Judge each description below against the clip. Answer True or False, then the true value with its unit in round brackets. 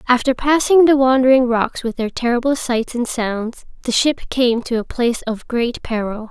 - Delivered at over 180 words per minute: True (190 wpm)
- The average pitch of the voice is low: False (245 Hz)